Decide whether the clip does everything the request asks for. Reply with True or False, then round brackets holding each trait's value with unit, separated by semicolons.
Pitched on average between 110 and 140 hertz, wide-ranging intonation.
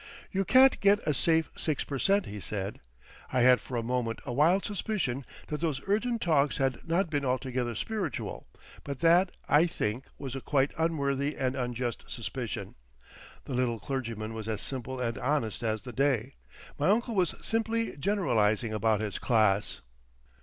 True (135 Hz; 6.0 semitones)